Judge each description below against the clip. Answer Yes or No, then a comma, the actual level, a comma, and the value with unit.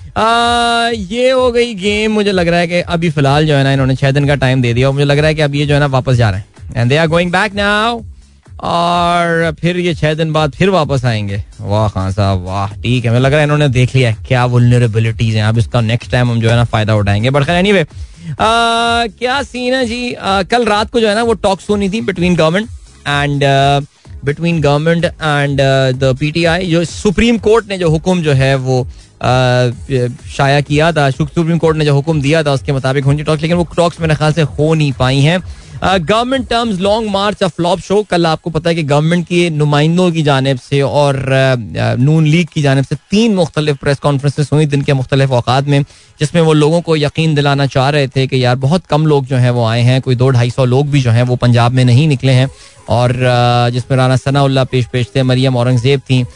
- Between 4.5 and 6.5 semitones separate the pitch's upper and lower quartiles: Yes, average, 5.1 semitones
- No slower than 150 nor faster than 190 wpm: Yes, average, 160 wpm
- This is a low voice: No, medium, 145 Hz